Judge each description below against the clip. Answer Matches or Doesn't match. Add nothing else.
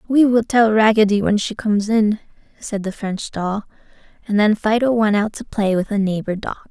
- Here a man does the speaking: Doesn't match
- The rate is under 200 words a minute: Doesn't match